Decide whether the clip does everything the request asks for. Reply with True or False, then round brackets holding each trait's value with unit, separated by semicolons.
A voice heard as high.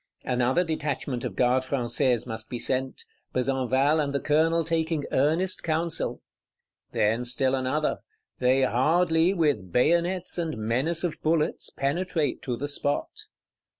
False (140 Hz)